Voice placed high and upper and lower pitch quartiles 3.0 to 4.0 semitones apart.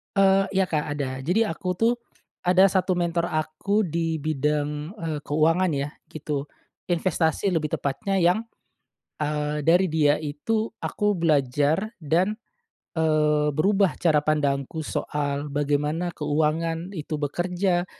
No: medium, 160 Hz; average, 3.3 semitones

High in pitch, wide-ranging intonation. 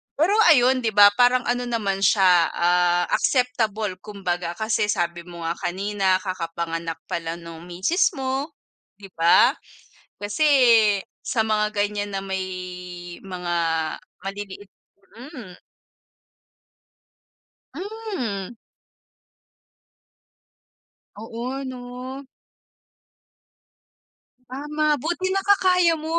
Yes: high, 210 Hz; wide, 6.2 semitones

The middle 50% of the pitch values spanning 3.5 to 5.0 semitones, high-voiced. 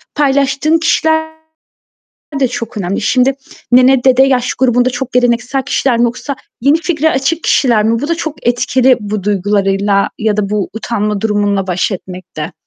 Yes: average, 4.4 semitones; high, 245 Hz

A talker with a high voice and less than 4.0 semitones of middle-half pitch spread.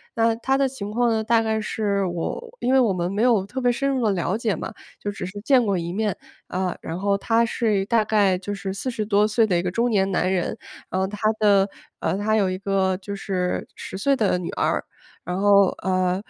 Yes: high, 205 Hz; average, 3.2 semitones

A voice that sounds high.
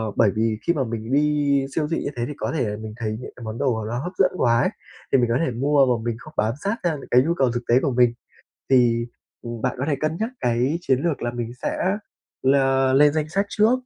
No: low, 130 Hz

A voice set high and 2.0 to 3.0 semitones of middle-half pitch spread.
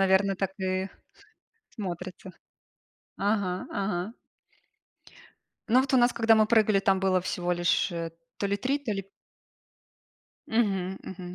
Yes: high, 195 Hz; average, 2.7 semitones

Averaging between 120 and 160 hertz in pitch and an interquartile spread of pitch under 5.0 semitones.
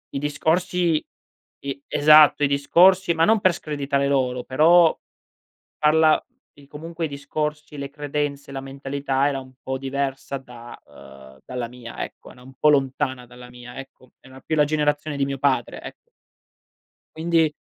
Yes: medium, 140 Hz; narrow, 2.6 semitones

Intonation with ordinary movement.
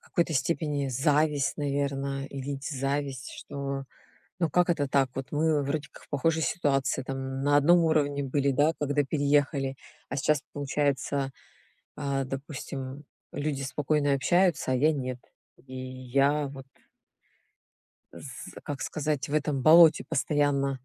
No: narrow, 1.7 semitones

